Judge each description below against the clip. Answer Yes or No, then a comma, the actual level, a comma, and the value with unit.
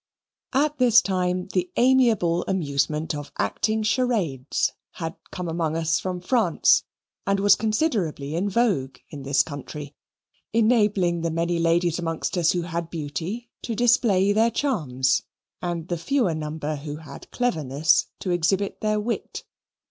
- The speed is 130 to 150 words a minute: Yes, average, 140 wpm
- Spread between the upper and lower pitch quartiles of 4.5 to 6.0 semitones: Yes, average, 5.3 semitones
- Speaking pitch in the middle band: Yes, medium, 175 Hz